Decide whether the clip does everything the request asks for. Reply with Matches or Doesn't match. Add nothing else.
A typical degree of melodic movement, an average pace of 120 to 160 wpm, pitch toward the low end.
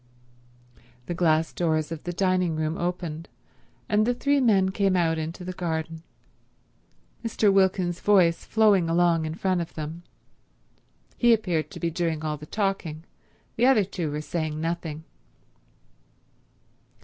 Doesn't match